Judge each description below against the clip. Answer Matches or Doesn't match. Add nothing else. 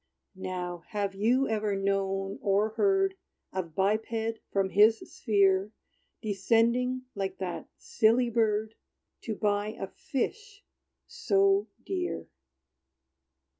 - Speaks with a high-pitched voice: Matches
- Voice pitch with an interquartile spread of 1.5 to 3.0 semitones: Doesn't match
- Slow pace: Matches